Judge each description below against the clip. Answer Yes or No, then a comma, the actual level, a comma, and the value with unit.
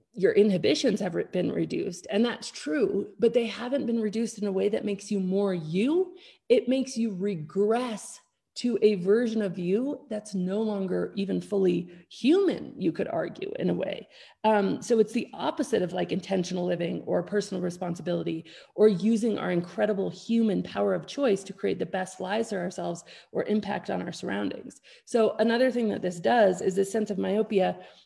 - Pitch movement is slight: No, average, 3.5 semitones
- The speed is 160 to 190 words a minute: Yes, average, 180 wpm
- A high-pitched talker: Yes, high, 205 Hz